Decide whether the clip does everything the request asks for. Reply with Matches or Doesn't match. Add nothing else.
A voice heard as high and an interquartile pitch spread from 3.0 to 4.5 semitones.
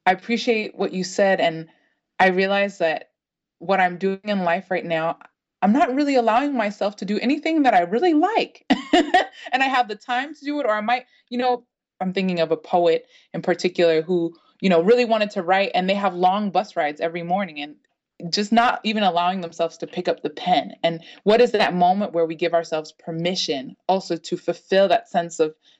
Doesn't match